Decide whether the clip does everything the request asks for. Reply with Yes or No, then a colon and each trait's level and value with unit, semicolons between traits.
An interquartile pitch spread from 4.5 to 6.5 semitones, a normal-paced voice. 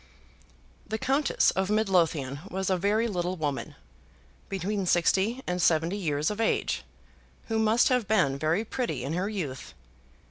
Yes: average, 4.9 semitones; average, 145 wpm